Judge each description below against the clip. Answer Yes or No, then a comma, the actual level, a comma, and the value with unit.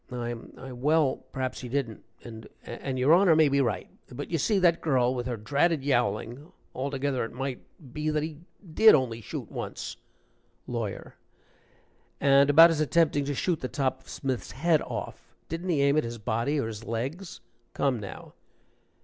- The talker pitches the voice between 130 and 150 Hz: Yes, low, 135 Hz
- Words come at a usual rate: Yes, average, 175 wpm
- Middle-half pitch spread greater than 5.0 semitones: No, average, 4.0 semitones